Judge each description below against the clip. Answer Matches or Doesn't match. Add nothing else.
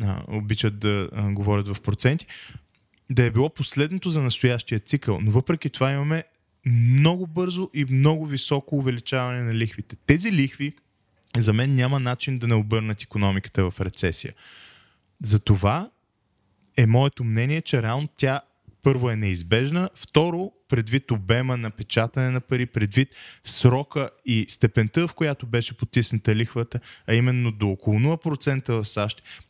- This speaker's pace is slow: Doesn't match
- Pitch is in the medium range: Doesn't match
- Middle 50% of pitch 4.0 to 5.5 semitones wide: Matches